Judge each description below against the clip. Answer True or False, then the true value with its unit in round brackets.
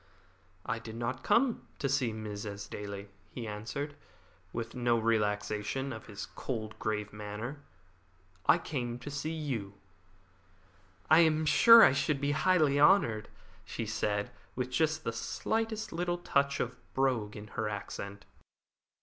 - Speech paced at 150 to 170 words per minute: False (140 wpm)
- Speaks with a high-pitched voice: False (120 Hz)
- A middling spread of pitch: False (5.8 semitones)